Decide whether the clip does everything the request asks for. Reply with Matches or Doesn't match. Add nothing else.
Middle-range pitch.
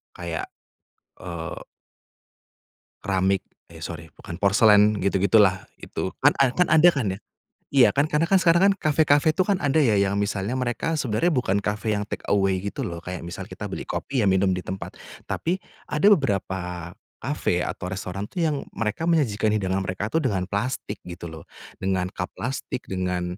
Doesn't match